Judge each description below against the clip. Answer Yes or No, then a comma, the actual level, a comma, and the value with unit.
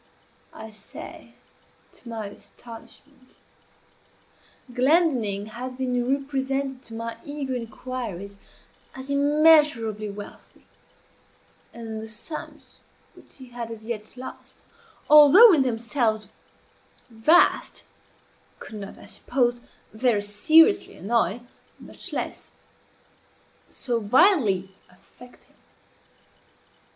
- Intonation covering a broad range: No, average, 3.9 semitones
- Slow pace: Yes, slow, 95 wpm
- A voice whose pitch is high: Yes, high, 240 Hz